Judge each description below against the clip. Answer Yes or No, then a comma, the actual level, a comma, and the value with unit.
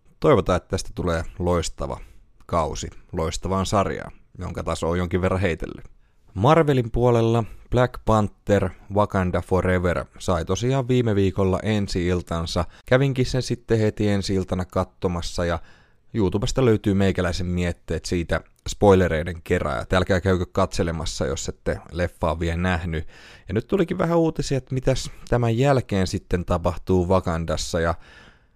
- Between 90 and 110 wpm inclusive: No, average, 130 wpm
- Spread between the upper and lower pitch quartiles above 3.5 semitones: Yes, average, 3.9 semitones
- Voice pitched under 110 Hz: Yes, very low, 95 Hz